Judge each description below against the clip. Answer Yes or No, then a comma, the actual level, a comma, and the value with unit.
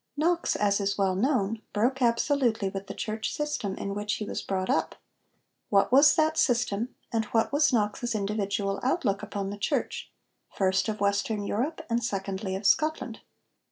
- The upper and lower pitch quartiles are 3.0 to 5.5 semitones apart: Yes, average, 4.2 semitones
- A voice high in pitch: Yes, high, 215 Hz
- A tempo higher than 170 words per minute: No, average, 165 wpm